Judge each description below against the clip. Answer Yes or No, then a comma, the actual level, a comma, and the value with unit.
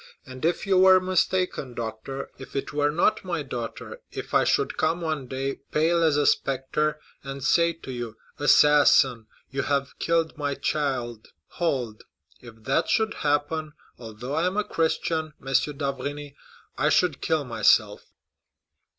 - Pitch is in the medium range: Yes, medium, 145 Hz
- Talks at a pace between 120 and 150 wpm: Yes, average, 140 wpm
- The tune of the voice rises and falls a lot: No, average, 3.6 semitones